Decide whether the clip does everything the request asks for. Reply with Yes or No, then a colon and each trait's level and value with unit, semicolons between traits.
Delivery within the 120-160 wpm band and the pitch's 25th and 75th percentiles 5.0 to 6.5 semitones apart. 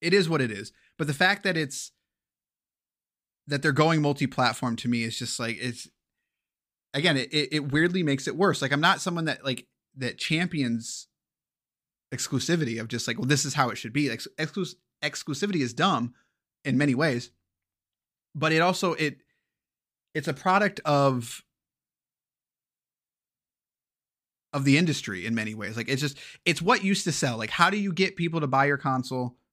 No: average, 175 wpm; average, 5.3 semitones